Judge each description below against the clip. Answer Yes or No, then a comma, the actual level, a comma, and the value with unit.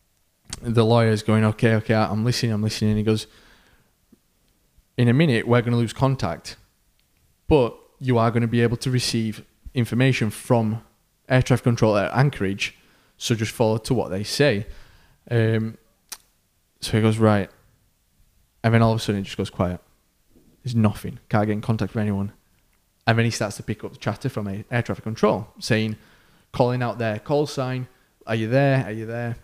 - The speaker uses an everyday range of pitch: No, narrow, 2.1 semitones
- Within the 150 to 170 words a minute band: No, average, 190 wpm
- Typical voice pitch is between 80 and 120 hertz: Yes, low, 110 Hz